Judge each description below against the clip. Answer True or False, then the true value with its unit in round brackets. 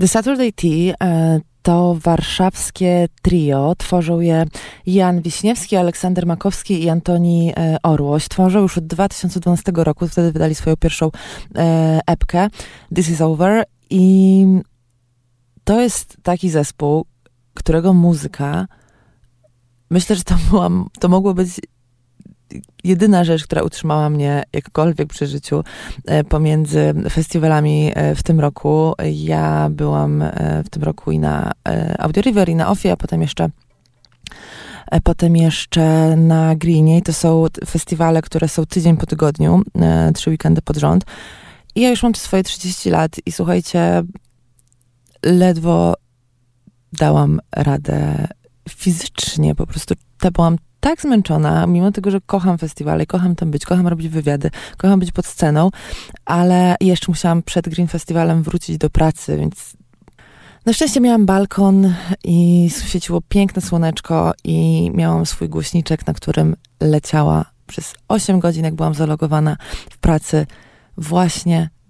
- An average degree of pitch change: True (3.8 semitones)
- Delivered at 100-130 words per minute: False (140 wpm)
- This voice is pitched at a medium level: True (165 Hz)